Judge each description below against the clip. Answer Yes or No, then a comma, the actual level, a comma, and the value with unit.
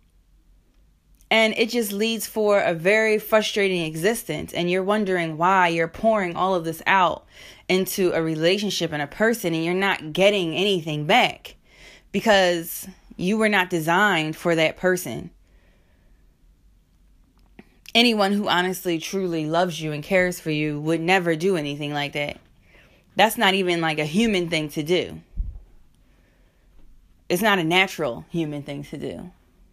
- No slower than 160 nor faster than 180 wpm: No, average, 145 wpm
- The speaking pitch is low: No, medium, 170 Hz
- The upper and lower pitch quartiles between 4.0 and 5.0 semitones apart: Yes, average, 4.7 semitones